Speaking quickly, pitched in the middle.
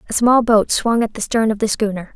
No: fast, 280 wpm; high, 220 Hz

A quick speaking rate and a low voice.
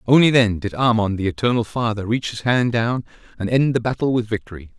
Yes: fast, 215 wpm; low, 115 Hz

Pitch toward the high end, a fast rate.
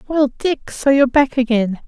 No: very high, 260 Hz; average, 190 wpm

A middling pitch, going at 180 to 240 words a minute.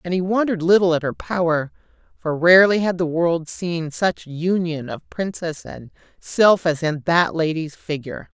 No: medium, 170 Hz; average, 170 wpm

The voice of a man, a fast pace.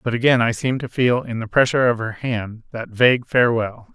Yes: male; fast, 230 wpm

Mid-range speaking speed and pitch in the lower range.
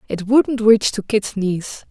No: average, 190 wpm; high, 215 Hz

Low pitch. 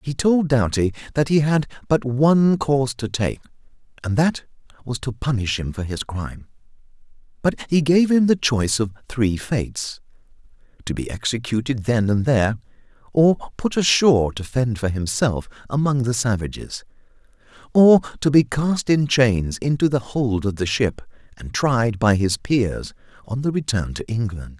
Yes: low, 125 Hz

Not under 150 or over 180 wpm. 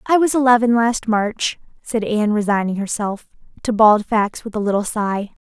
Yes: average, 175 wpm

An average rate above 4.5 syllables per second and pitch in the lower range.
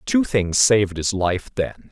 No: 3.9 syllables/s; low, 105 Hz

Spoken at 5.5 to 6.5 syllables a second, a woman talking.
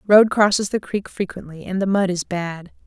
No: 5.0 syllables/s; female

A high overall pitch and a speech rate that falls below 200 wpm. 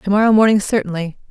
Yes: high, 200 Hz; average, 140 wpm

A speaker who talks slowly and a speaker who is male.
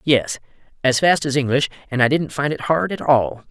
No: fast, 205 wpm; male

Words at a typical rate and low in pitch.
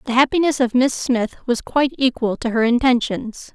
No: average, 185 wpm; very high, 250 Hz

